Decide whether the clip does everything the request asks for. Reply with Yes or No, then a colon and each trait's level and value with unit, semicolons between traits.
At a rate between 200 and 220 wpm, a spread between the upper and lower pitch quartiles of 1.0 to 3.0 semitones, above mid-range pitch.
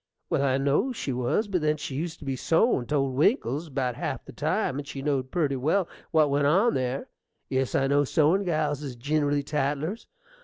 No: fast, 205 wpm; average, 2.7 semitones; medium, 145 Hz